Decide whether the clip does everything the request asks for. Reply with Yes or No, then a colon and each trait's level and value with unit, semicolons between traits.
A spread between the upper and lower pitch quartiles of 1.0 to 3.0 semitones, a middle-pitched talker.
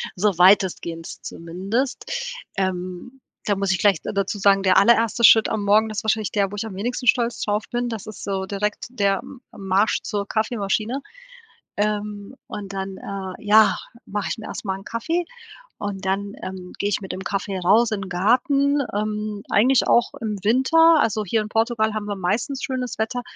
No: average, 2.7 semitones; high, 210 Hz